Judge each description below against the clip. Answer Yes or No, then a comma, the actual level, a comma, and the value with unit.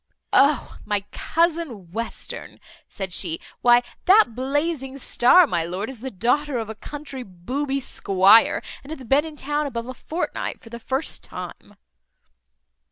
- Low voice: No, very high, 255 Hz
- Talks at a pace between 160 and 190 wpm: No, average, 150 wpm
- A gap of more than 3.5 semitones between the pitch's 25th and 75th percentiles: Yes, average, 5.1 semitones